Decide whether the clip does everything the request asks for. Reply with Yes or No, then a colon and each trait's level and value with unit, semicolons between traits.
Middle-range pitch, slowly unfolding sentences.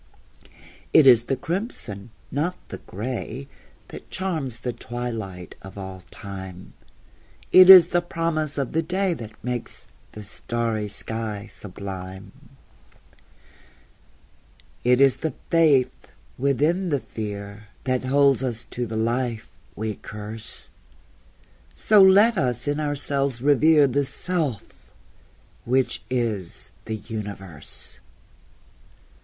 No: low, 125 Hz; slow, 110 wpm